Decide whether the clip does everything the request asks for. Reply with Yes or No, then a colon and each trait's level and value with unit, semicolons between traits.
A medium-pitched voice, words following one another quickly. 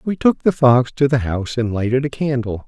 No: low, 130 Hz; fast, 245 wpm